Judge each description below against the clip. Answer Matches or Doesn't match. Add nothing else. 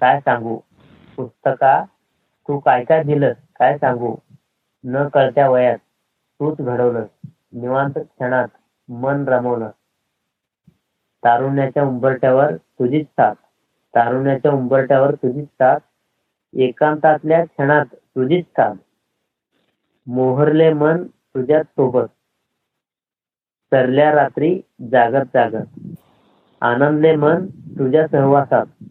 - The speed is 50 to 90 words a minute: Matches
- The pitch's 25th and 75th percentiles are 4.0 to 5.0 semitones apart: Doesn't match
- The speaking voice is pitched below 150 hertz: Matches